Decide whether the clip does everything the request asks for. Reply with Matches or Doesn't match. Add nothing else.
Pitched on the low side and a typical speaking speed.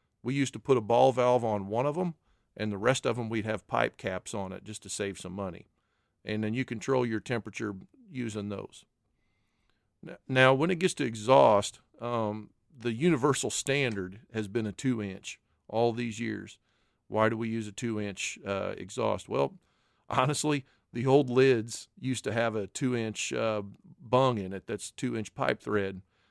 Matches